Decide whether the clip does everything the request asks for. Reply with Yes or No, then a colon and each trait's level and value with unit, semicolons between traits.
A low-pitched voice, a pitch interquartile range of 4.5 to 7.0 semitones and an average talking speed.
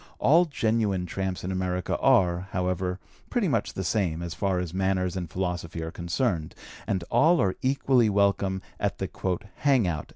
No: very low, 95 Hz; narrow, 2.4 semitones; average, 165 wpm